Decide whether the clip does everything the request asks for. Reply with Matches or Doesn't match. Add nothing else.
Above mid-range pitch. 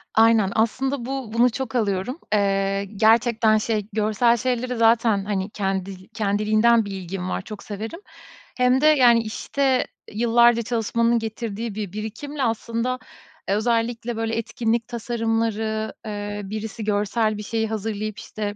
Matches